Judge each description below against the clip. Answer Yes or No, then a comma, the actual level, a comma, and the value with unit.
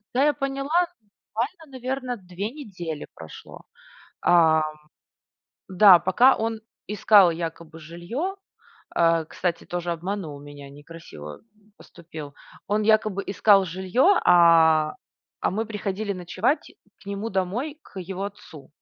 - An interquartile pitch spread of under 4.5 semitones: No, average, 5.1 semitones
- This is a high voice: Yes, high, 195 Hz